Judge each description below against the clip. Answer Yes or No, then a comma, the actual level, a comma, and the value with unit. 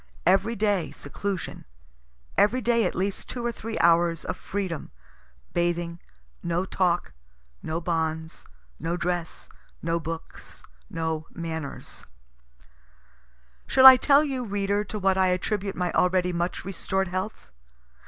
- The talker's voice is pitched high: No, medium, 180 Hz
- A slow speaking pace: Yes, slow, 125 wpm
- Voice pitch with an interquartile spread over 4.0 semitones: No, average, 3.2 semitones